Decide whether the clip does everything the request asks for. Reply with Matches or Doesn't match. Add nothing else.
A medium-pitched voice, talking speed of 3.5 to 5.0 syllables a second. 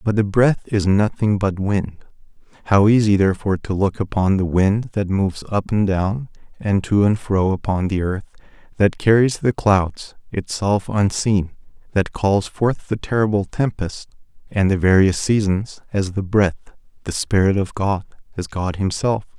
Doesn't match